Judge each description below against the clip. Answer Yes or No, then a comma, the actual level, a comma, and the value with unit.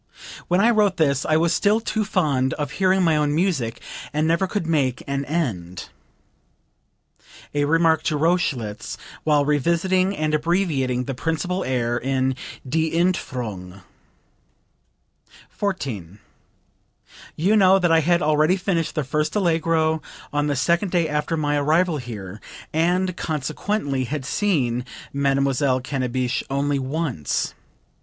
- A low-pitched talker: No, medium, 155 Hz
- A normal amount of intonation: Yes, average, 4.6 semitones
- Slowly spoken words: Yes, slow, 130 wpm